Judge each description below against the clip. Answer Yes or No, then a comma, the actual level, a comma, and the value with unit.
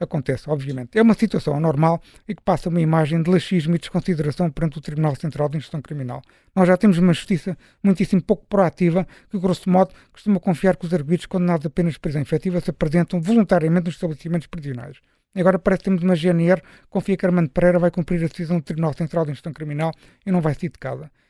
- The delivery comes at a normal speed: No, fast, 215 wpm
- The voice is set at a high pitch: No, medium, 175 Hz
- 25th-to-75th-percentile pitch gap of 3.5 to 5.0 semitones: No, average, 2.7 semitones